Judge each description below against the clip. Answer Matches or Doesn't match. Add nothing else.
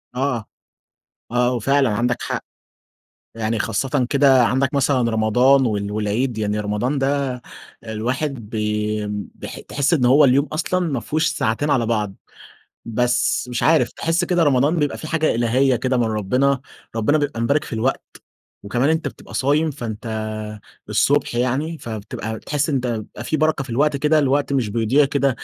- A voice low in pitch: Matches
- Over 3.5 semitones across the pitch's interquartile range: Matches